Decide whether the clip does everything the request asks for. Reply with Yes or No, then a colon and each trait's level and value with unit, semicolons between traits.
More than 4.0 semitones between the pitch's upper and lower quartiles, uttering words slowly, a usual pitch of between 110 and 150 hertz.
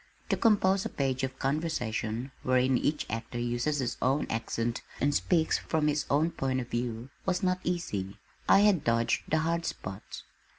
No: average, 5.1 semitones; average, 170 wpm; low, 135 Hz